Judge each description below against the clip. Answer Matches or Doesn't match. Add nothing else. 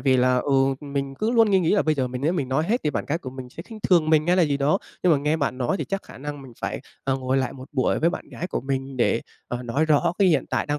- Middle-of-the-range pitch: Matches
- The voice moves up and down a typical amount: Matches